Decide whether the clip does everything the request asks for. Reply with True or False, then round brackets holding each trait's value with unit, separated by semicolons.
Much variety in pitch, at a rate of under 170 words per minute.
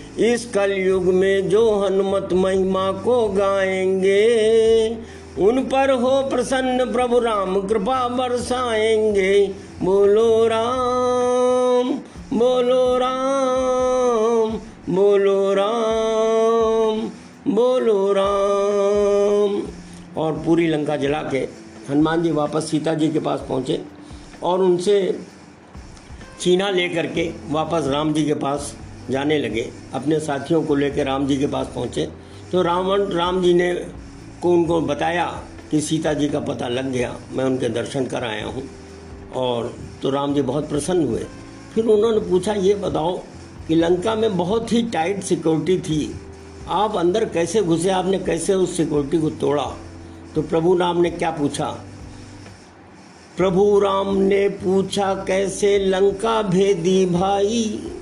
True (6.6 semitones; 125 wpm)